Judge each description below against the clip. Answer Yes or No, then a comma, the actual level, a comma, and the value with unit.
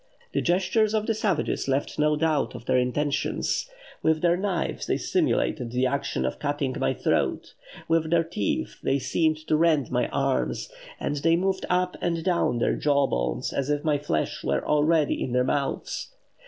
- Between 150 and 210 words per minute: Yes, average, 175 wpm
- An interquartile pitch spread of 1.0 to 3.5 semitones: No, average, 4.2 semitones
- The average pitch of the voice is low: No, medium, 150 Hz